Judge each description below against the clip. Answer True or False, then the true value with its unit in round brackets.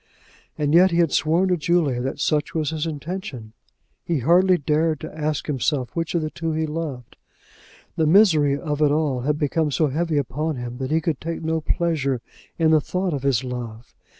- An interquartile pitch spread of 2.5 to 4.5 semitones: True (3.0 semitones)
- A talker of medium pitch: True (155 Hz)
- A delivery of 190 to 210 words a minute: True (200 wpm)